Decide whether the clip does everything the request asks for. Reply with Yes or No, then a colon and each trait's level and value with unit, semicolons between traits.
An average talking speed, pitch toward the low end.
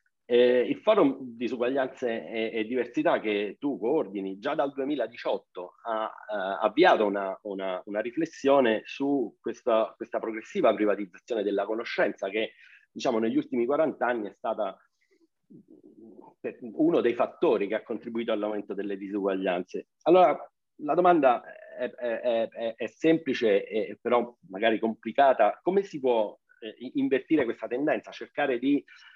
Yes: average, 135 wpm; low, 120 Hz